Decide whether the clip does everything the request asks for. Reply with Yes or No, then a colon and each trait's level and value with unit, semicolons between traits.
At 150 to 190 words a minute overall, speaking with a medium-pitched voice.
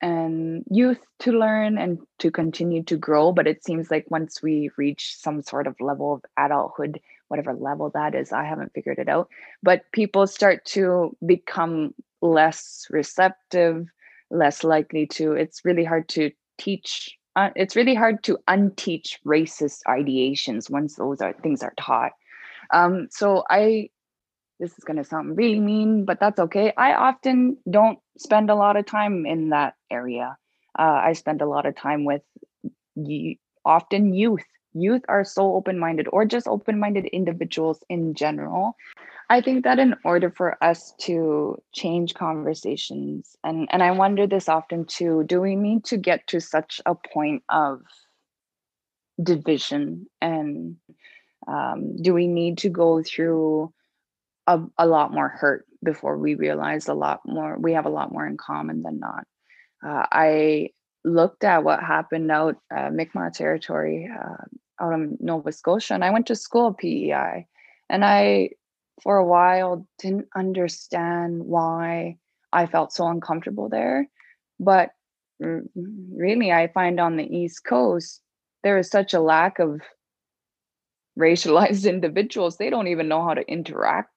Yes: average, 155 wpm; medium, 170 Hz